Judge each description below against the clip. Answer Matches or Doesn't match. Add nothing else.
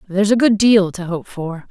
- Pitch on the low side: Doesn't match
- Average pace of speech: Doesn't match